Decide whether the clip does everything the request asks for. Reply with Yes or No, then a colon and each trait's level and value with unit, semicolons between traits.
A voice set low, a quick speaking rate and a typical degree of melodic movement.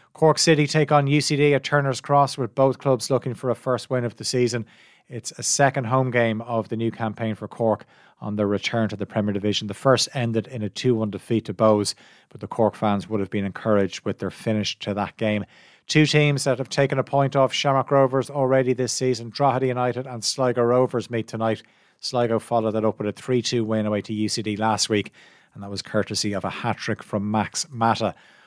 Yes: low, 115 Hz; fast, 215 wpm; average, 3.8 semitones